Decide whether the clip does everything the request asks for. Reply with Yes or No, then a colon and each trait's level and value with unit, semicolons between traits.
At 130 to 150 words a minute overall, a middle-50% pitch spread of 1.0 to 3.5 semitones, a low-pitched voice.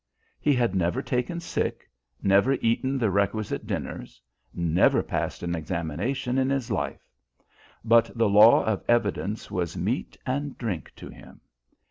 No: average, 140 wpm; average, 5.3 semitones; low, 115 Hz